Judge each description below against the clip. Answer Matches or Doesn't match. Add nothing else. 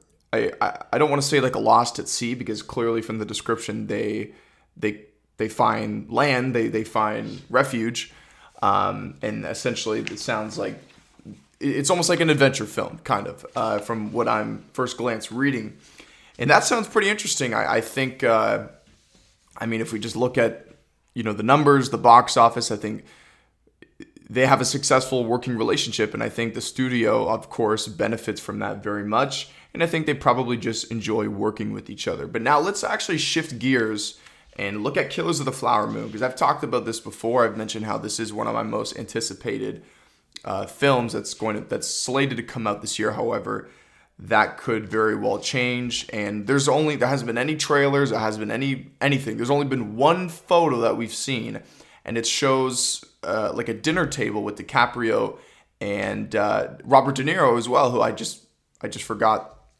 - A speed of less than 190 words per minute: Doesn't match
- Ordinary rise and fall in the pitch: Matches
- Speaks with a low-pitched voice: Matches